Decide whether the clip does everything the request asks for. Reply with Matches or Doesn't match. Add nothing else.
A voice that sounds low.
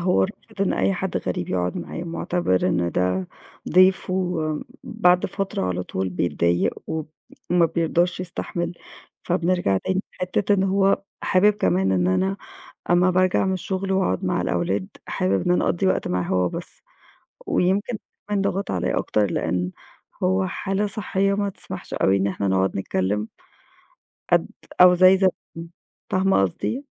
Doesn't match